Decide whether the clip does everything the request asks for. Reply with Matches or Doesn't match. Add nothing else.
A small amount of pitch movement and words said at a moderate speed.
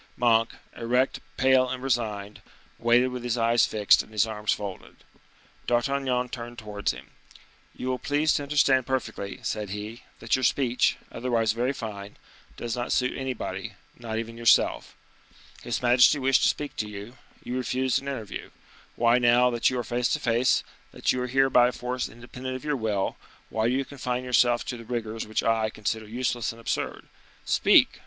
Matches